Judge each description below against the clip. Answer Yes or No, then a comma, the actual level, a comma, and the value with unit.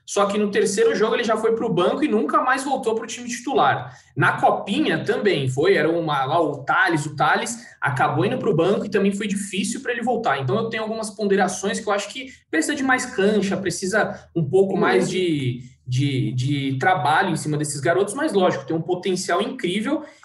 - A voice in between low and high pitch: No, high, 200 Hz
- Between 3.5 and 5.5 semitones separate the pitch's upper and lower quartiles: Yes, average, 5.1 semitones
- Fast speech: Yes, fast, 215 wpm